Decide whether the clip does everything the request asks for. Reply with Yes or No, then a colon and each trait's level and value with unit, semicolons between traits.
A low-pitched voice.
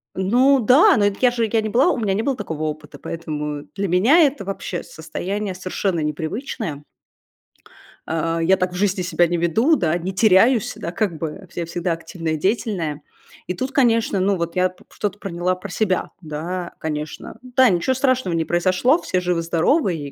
No: medium, 185 Hz